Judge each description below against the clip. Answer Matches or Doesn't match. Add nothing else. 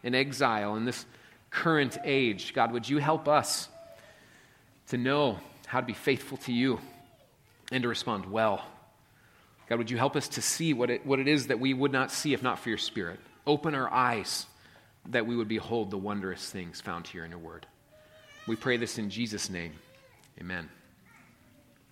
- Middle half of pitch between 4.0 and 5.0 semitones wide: Matches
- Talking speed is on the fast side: Doesn't match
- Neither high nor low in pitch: Doesn't match